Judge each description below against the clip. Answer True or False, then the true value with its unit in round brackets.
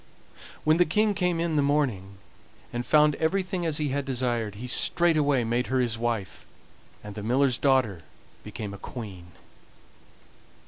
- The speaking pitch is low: True (130 Hz)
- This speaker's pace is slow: False (150 wpm)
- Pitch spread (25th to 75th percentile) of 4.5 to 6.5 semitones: True (5.4 semitones)